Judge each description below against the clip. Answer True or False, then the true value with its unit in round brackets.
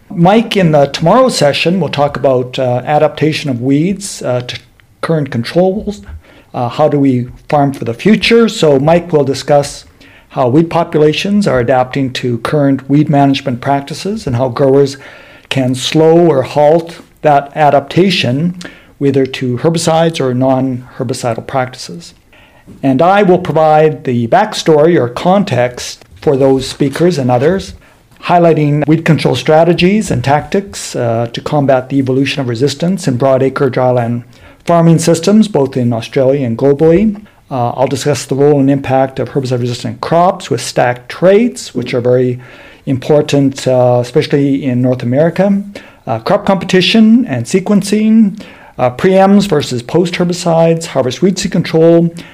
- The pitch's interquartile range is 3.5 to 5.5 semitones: True (4.7 semitones)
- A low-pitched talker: False (145 Hz)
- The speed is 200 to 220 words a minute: False (145 wpm)